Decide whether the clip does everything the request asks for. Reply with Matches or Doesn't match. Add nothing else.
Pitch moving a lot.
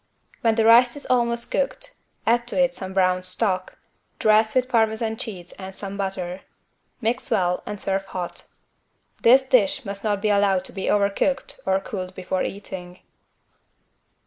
Doesn't match